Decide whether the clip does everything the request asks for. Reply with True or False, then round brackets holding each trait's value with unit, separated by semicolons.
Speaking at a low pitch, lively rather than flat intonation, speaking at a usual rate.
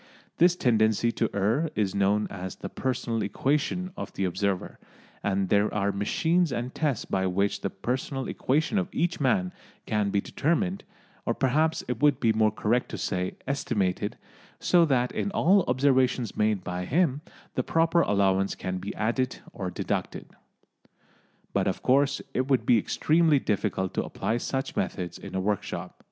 True (115 Hz; 6.2 semitones; 165 wpm)